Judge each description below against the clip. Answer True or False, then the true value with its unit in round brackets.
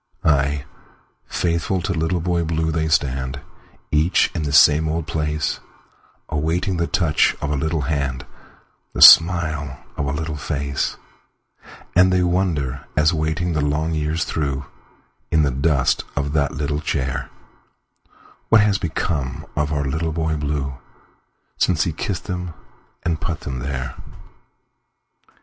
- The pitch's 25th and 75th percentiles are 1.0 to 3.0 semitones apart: True (2.7 semitones)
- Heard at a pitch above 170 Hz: False (75 Hz)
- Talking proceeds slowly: True (125 wpm)